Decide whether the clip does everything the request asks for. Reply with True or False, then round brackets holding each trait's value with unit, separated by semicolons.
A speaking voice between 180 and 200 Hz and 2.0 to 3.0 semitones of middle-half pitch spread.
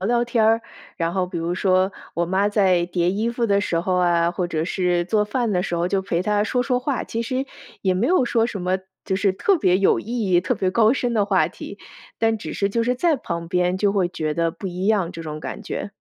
False (190 Hz; 4.2 semitones)